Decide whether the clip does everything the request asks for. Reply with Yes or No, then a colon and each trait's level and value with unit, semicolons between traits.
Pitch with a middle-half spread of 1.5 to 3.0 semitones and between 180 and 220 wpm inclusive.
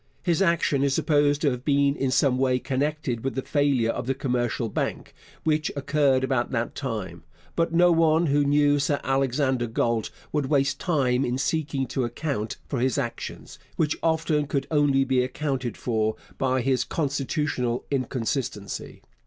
No: average, 2.7 semitones; average, 160 wpm